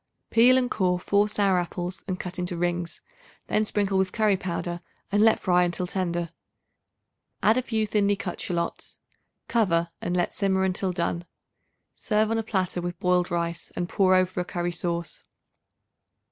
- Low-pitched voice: No, medium, 185 Hz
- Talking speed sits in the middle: Yes, average, 165 wpm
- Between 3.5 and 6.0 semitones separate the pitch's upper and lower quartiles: No, average, 2.7 semitones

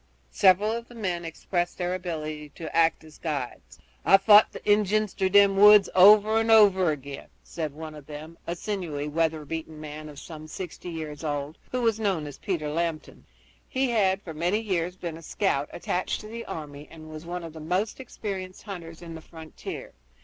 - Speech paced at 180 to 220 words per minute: Yes, average, 195 wpm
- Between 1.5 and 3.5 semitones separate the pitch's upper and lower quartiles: No, average, 4.3 semitones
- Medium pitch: Yes, medium, 170 Hz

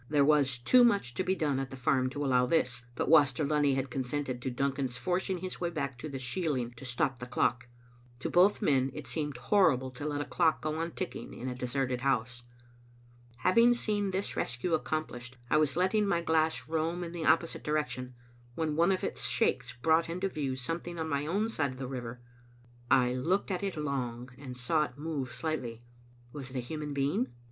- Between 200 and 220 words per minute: Yes, fast, 205 wpm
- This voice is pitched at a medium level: Yes, medium, 145 Hz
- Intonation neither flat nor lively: Yes, average, 4.5 semitones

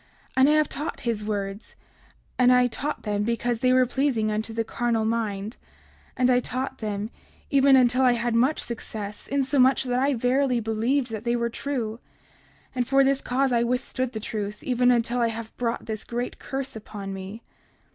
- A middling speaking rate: Yes, average, 185 wpm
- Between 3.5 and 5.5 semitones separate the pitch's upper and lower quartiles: No, average, 2.8 semitones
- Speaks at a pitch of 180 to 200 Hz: No, high, 240 Hz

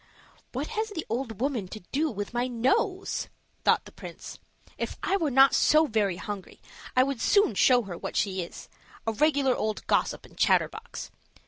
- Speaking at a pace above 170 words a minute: Yes, average, 180 wpm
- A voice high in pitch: Yes, very high, 255 Hz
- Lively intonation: Yes, wide, 6.3 semitones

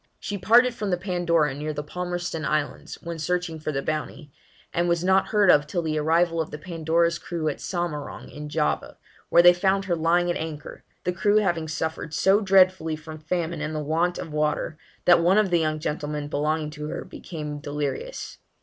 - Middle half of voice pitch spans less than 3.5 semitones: Yes, average, 2.7 semitones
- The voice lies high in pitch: No, medium, 165 Hz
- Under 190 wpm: No, average, 195 wpm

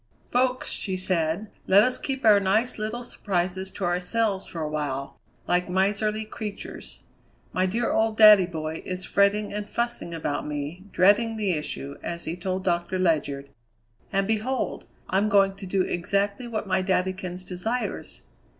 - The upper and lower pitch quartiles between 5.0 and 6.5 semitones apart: No, average, 3.3 semitones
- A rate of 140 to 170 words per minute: Yes, average, 155 wpm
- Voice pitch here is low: No, high, 190 Hz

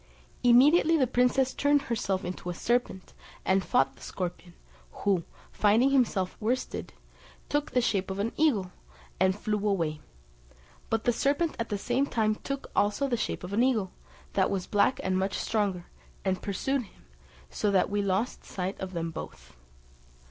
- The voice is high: Yes, high, 205 Hz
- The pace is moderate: Yes, average, 165 wpm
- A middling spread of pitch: Yes, average, 4.8 semitones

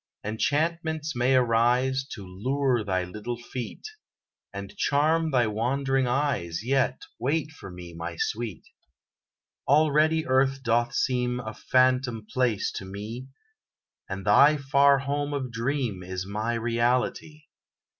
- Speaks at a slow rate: Yes, slow, 125 wpm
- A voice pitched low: Yes, low, 125 Hz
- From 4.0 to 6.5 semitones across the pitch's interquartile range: Yes, average, 4.3 semitones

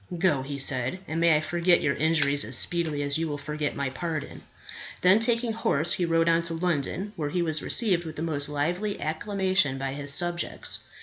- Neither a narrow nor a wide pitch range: Yes, average, 3.4 semitones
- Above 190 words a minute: Yes, average, 200 wpm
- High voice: No, medium, 160 Hz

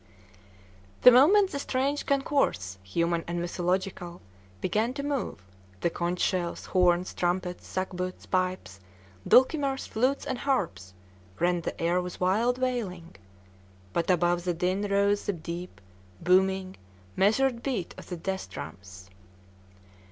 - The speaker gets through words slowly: Yes, slow, 125 wpm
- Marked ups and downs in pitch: Yes, wide, 6.1 semitones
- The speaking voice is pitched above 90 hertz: Yes, medium, 185 Hz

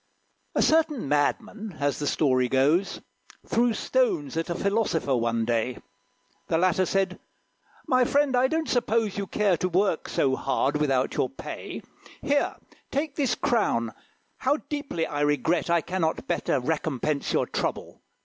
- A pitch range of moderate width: No, wide, 8.9 semitones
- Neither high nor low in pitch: Yes, medium, 180 Hz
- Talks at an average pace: Yes, average, 150 wpm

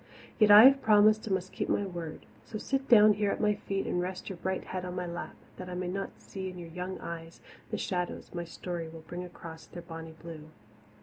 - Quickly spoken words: Yes, fast, 235 wpm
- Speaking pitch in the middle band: Yes, medium, 180 Hz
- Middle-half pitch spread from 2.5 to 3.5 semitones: Yes, average, 3.0 semitones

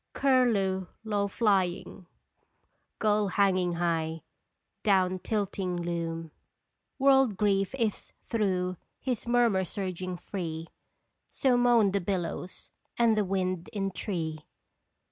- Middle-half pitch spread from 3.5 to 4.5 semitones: No, average, 3.1 semitones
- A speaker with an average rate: No, slow, 105 wpm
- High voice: Yes, high, 195 Hz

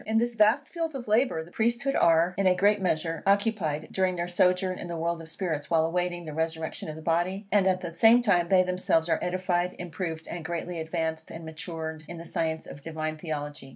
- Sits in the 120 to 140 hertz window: No, medium, 175 Hz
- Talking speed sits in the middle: No, fast, 220 wpm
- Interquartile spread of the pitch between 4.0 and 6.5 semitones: No, average, 2.9 semitones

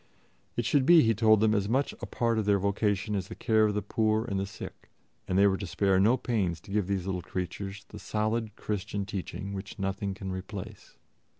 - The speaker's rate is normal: No, fast, 220 wpm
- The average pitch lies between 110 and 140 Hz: No, low, 100 Hz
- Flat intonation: Yes, narrow, 2.0 semitones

